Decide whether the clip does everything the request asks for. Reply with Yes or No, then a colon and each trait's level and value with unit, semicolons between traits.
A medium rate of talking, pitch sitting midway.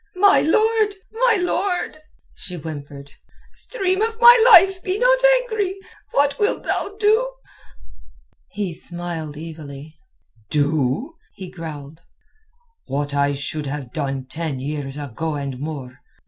No: slow, 120 wpm; medium, 165 Hz